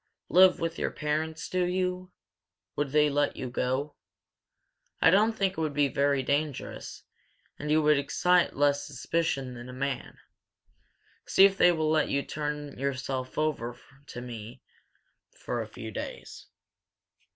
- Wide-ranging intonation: No, average, 3.7 semitones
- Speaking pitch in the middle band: Yes, medium, 145 Hz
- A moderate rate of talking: Yes, average, 150 wpm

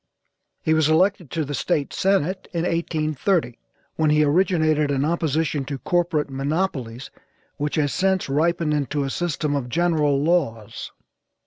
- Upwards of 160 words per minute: No, average, 140 wpm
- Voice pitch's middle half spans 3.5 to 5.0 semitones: No, average, 3.1 semitones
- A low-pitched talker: No, medium, 155 Hz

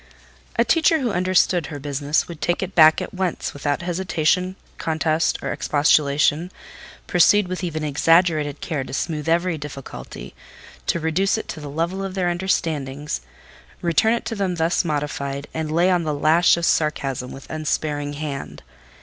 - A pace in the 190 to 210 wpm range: No, average, 160 wpm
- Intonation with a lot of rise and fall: No, average, 3.4 semitones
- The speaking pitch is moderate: Yes, medium, 160 Hz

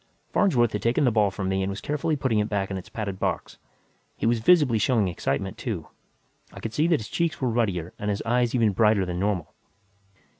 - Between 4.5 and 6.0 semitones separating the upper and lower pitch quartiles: No, average, 4.0 semitones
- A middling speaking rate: No, fast, 220 wpm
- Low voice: Yes, low, 110 Hz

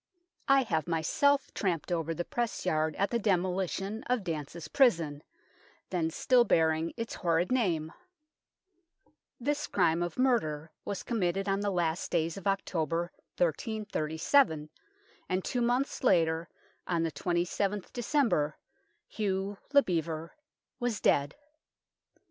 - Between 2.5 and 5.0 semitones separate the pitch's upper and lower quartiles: No, wide, 5.4 semitones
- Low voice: No, medium, 180 Hz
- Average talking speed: No, slow, 125 wpm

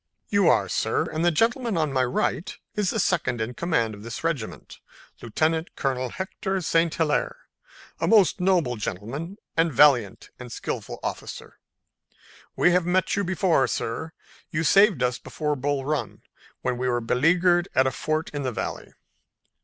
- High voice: No, medium, 160 Hz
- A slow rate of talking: No, average, 160 wpm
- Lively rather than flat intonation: Yes, wide, 5.9 semitones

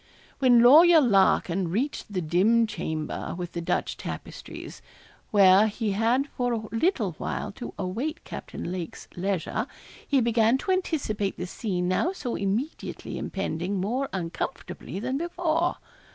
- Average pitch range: No, wide, 6.0 semitones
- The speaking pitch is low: No, high, 220 Hz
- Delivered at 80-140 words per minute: Yes, slow, 135 wpm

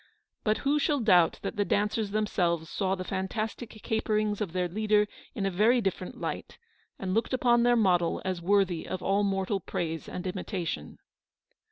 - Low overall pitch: No, high, 200 Hz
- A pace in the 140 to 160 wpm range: No, average, 175 wpm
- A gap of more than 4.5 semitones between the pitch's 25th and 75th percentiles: No, average, 2.9 semitones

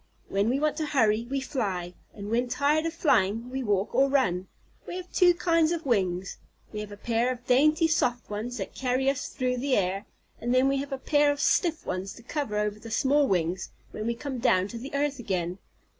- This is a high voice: Yes, very high, 250 Hz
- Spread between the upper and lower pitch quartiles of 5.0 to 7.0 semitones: Yes, average, 5.3 semitones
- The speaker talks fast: Yes, fast, 220 wpm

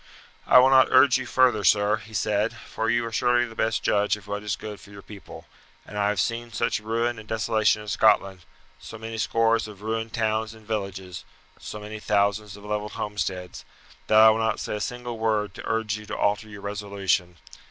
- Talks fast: Yes, fast, 210 wpm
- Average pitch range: No, narrow, 1.6 semitones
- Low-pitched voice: Yes, low, 105 Hz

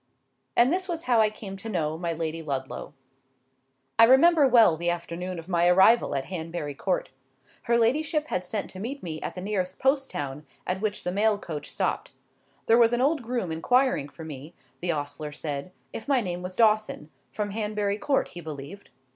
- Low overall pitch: No, high, 190 Hz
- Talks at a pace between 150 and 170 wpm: No, average, 190 wpm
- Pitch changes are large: Yes, wide, 6.4 semitones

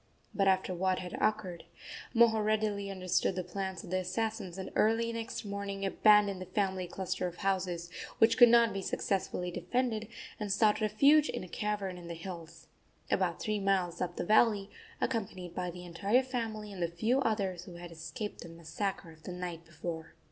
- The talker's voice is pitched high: Yes, high, 195 Hz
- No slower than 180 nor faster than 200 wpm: Yes, average, 185 wpm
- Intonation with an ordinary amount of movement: Yes, average, 3.2 semitones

